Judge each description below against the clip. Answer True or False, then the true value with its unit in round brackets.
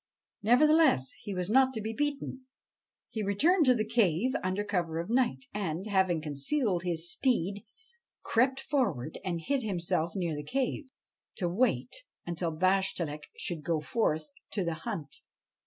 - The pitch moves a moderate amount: False (6.9 semitones)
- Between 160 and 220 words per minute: False (150 wpm)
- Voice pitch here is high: True (195 Hz)